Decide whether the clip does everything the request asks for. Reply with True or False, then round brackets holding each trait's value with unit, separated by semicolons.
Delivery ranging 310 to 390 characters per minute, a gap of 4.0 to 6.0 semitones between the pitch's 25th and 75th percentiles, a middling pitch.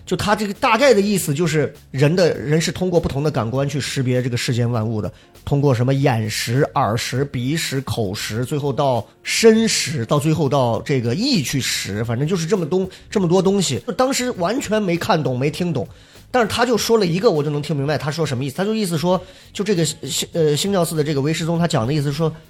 True (330 characters per minute; 5.5 semitones; 155 Hz)